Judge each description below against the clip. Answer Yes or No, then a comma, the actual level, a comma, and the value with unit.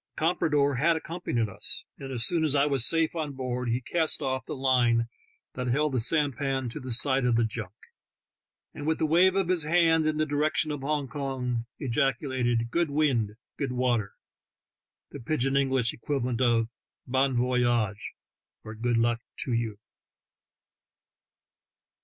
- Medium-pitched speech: No, low, 130 Hz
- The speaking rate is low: No, average, 170 wpm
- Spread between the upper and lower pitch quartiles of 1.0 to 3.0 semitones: No, average, 3.9 semitones